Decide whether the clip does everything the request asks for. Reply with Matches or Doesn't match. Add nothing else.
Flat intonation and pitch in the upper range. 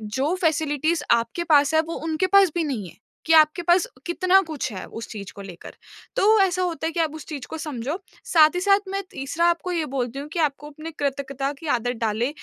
Doesn't match